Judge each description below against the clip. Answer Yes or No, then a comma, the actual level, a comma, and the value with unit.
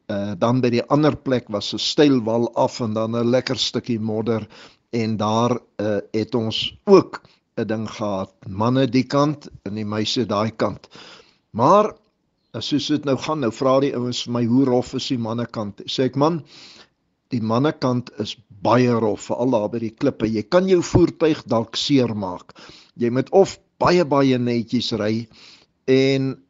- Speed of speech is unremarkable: Yes, average, 175 wpm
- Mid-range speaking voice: No, low, 120 Hz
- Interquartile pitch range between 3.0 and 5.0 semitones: Yes, average, 3.4 semitones